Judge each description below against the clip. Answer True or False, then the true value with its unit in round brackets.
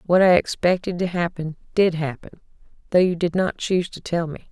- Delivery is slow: False (200 wpm)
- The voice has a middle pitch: True (175 Hz)